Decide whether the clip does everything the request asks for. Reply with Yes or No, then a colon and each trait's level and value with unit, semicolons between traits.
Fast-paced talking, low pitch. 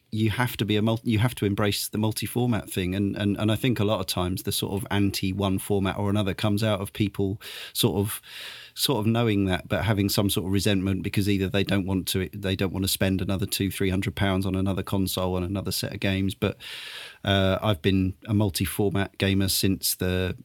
Yes: fast, 230 wpm; low, 100 Hz